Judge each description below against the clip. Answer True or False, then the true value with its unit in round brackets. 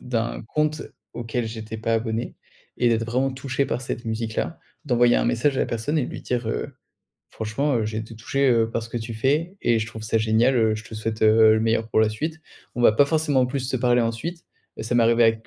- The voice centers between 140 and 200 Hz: False (115 Hz)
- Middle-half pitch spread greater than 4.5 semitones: False (2.7 semitones)